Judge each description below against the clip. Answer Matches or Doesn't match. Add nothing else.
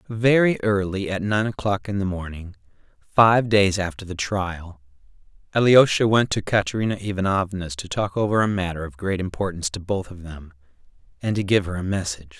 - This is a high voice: Doesn't match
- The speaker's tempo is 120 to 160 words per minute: Doesn't match